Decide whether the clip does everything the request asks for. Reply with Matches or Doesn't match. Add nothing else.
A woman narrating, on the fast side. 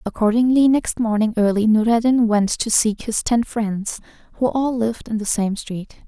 Doesn't match